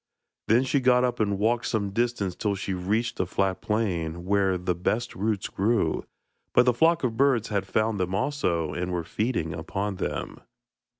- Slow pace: No, average, 185 wpm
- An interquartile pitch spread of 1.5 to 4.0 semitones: No, average, 4.4 semitones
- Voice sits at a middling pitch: No, low, 100 Hz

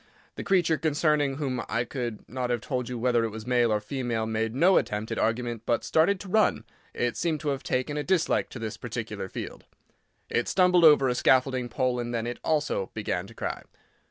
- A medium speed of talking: No, fast, 210 wpm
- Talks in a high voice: No, low, 125 Hz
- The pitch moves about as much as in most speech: Yes, average, 4.3 semitones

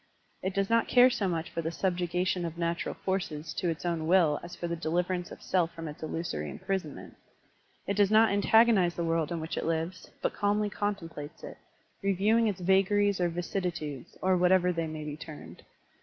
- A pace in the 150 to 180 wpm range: No, average, 195 wpm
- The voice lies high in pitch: No, medium, 175 Hz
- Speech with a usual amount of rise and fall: Yes, average, 3.0 semitones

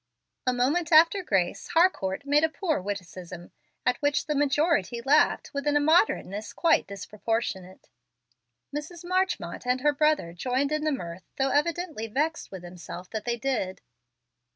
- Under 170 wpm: Yes, average, 150 wpm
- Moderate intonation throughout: No, wide, 7.7 semitones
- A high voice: Yes, very high, 270 Hz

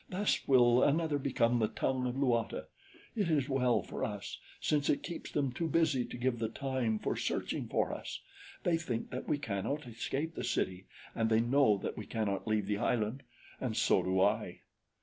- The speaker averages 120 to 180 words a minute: No, average, 190 wpm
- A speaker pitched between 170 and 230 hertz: No, low, 125 Hz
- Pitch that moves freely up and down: No, average, 4.3 semitones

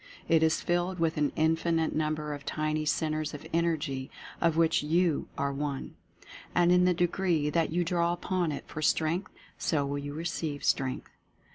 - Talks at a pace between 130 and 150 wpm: No, average, 170 wpm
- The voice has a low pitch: No, medium, 160 Hz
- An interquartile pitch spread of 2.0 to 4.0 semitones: Yes, narrow, 2.4 semitones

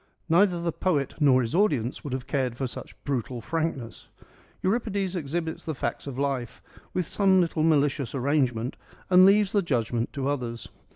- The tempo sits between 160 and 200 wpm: Yes, average, 165 wpm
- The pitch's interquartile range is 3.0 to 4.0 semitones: No, average, 5.3 semitones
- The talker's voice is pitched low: No, medium, 145 Hz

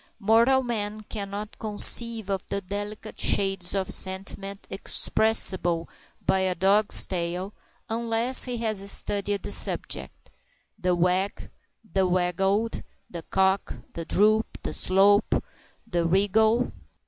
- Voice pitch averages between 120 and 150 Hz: No, high, 200 Hz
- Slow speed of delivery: Yes, slow, 115 wpm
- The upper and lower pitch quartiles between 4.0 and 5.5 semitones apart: No, narrow, 2.4 semitones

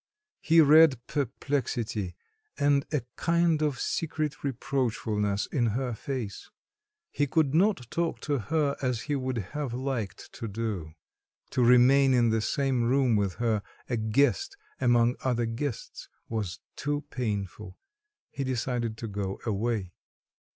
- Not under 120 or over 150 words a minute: Yes, slow, 135 wpm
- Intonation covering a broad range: No, average, 4.3 semitones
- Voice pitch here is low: Yes, low, 125 Hz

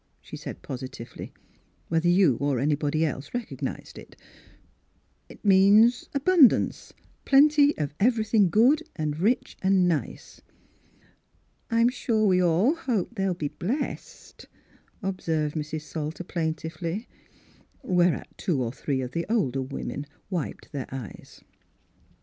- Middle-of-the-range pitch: Yes, medium, 175 Hz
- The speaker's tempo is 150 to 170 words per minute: No, slow, 135 wpm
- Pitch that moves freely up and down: Yes, wide, 6.8 semitones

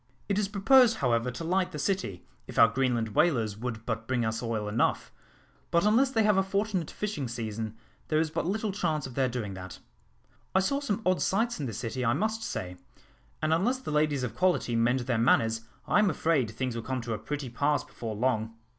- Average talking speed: No, fast, 215 wpm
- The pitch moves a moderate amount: No, wide, 8.8 semitones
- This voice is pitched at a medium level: No, low, 130 Hz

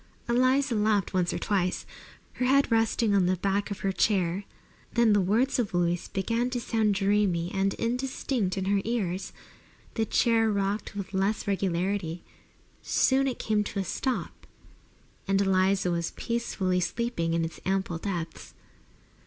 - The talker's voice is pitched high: Yes, high, 200 Hz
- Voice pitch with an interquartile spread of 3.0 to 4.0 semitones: Yes, average, 3.7 semitones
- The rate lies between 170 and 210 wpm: No, average, 155 wpm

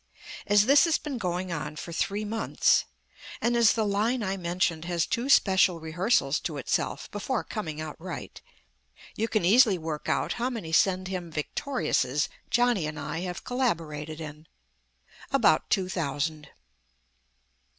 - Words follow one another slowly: No, average, 150 wpm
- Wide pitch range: Yes, wide, 5.7 semitones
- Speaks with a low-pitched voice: No, medium, 180 Hz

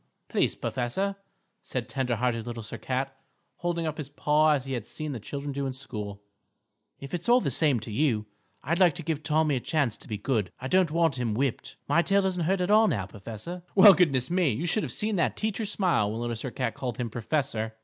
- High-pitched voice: No, medium, 140 Hz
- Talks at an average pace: No, fast, 230 wpm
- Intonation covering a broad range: Yes, wide, 6.3 semitones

